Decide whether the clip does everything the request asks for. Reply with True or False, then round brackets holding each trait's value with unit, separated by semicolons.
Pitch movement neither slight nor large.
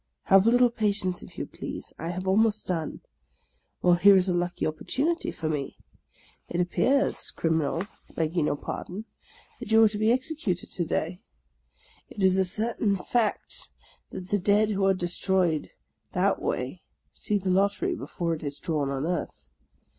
True (3.7 semitones)